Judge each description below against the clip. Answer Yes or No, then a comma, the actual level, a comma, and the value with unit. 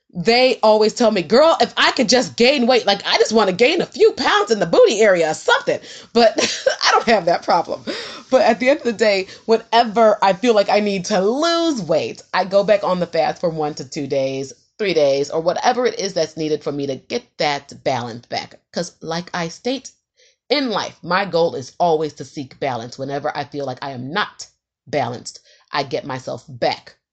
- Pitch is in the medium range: No, high, 205 Hz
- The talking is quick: Yes, fast, 220 wpm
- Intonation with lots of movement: Yes, wide, 7.3 semitones